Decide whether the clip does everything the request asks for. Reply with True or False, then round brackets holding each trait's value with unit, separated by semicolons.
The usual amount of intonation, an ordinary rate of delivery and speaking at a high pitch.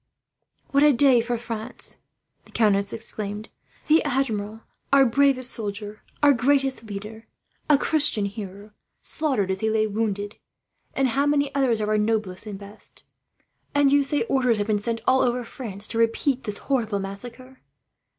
True (4.4 semitones; 160 wpm; 230 Hz)